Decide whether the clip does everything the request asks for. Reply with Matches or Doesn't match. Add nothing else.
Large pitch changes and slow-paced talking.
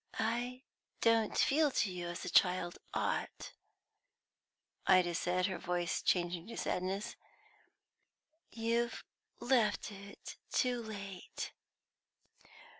Doesn't match